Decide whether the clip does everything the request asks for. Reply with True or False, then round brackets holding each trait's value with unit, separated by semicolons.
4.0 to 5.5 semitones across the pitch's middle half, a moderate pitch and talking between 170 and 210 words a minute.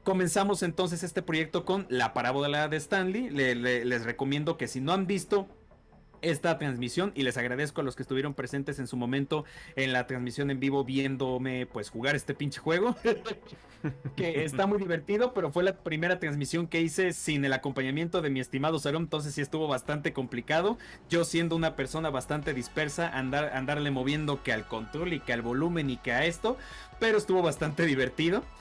True (4.3 semitones; 150 Hz; 185 wpm)